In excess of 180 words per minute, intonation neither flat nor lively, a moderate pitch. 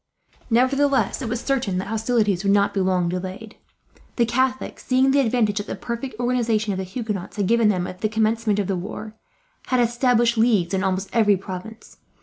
No: average, 190 wpm; average, 3.6 semitones; high, 220 Hz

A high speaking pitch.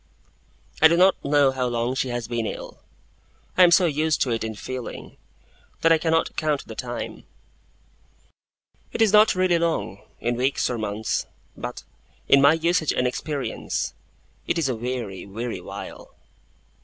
No: low, 135 Hz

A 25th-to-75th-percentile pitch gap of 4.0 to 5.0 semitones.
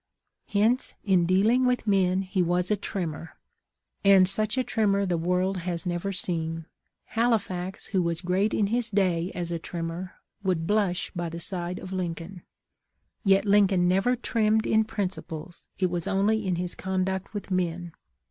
No: narrow, 2.6 semitones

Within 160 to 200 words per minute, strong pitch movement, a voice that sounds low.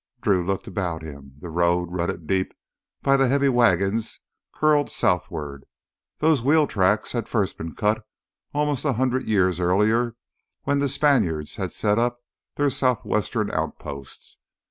No: average, 145 wpm; wide, 7.1 semitones; low, 105 Hz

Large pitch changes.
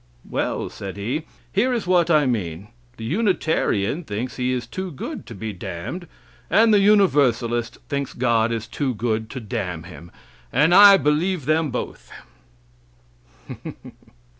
Yes: wide, 7.7 semitones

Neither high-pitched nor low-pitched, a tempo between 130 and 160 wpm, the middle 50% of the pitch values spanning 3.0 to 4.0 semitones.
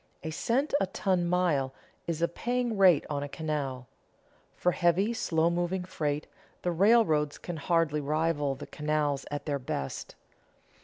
Yes: medium, 160 Hz; average, 150 wpm; average, 3.6 semitones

